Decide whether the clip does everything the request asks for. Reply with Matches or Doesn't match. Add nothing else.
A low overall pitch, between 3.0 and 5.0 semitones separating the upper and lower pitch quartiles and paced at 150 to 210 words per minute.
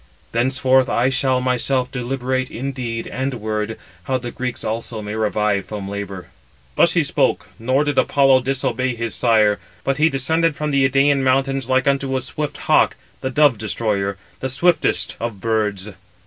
Matches